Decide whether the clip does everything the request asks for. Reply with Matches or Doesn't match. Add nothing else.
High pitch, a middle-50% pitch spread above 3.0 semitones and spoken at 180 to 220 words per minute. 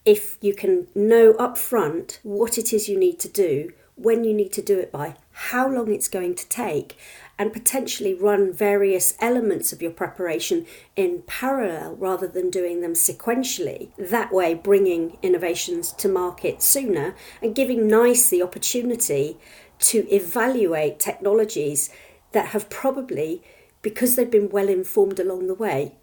Doesn't match